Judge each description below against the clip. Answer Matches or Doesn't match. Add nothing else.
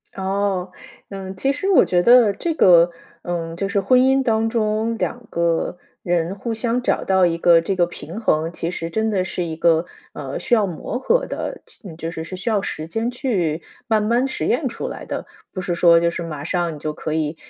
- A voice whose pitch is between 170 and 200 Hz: Matches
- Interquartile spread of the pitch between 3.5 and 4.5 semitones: Doesn't match